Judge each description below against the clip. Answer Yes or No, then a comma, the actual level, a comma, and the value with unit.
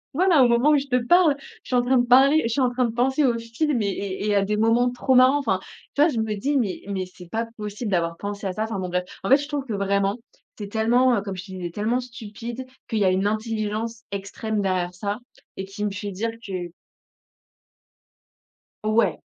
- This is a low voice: No, high, 220 Hz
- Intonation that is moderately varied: Yes, average, 3.9 semitones